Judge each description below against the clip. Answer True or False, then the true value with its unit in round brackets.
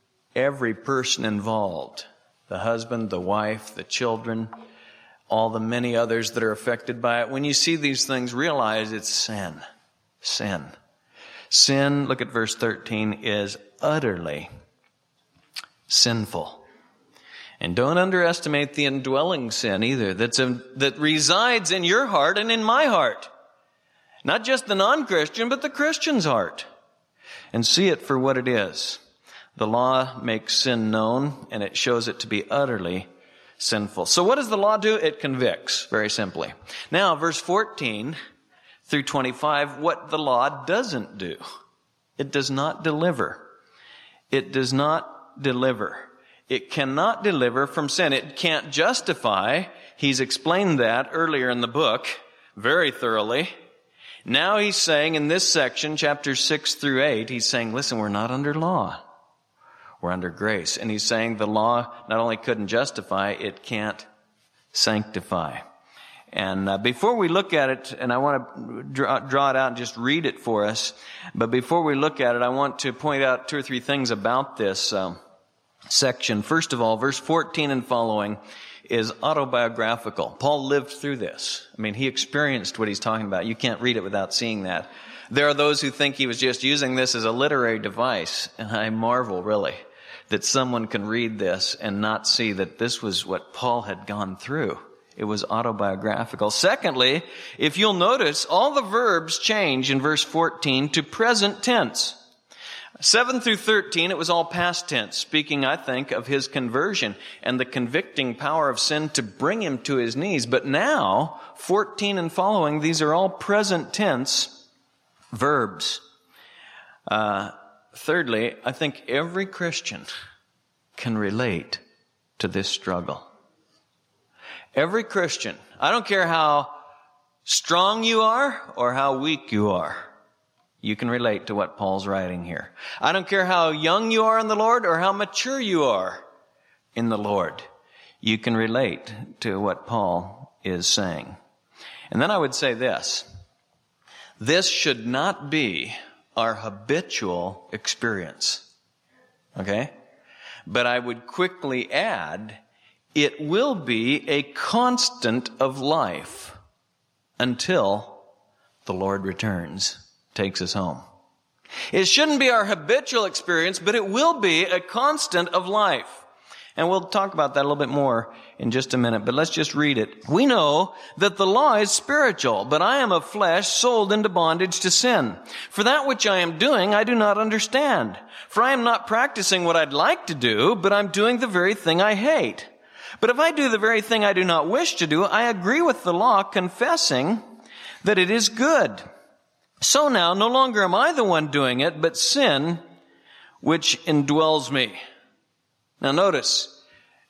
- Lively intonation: True (8.1 semitones)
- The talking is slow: False (160 wpm)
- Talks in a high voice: False (140 Hz)